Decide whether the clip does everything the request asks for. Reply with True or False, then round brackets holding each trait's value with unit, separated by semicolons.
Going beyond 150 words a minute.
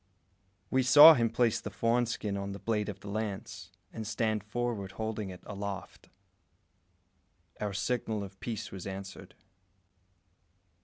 False (140 wpm)